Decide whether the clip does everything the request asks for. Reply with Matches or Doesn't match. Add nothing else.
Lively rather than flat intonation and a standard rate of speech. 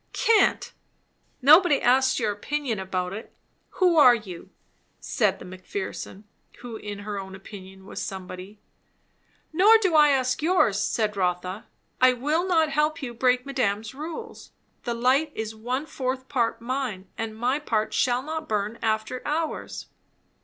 Matches